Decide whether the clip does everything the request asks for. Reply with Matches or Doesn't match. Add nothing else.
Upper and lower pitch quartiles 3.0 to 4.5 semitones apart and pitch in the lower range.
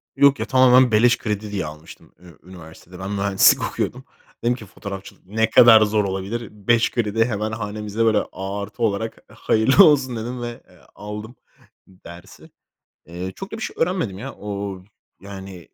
Matches